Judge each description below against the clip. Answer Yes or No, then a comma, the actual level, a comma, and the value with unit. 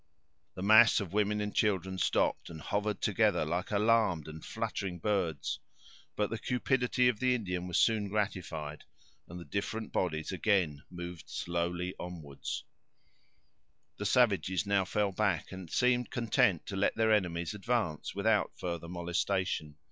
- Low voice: Yes, very low, 95 Hz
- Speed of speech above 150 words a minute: No, average, 145 wpm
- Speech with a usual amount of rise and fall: Yes, average, 3.5 semitones